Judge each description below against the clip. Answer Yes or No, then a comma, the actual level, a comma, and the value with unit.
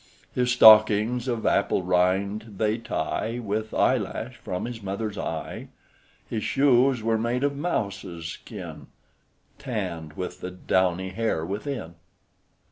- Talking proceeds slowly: Yes, slow, 125 wpm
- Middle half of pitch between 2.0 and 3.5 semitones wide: No, average, 4.4 semitones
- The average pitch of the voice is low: Yes, low, 110 Hz